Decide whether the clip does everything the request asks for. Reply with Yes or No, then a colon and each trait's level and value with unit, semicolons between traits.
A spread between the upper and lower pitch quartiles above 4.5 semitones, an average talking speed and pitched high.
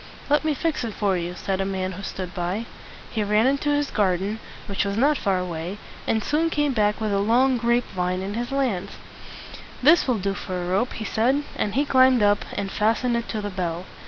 No: average, 4.9 semitones; fast, 220 wpm; high, 210 Hz